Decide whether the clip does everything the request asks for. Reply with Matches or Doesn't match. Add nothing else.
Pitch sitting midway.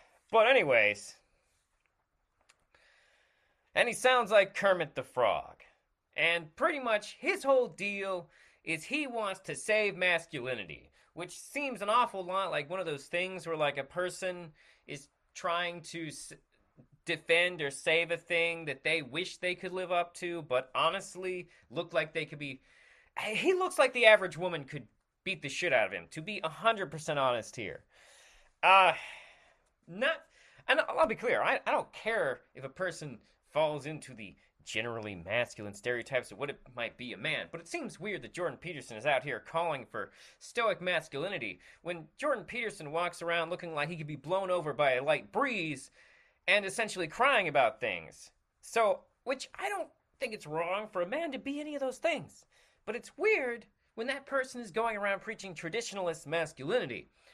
Matches